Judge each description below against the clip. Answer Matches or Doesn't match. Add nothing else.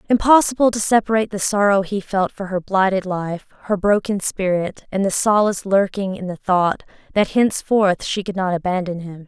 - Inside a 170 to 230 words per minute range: Matches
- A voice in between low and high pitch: Doesn't match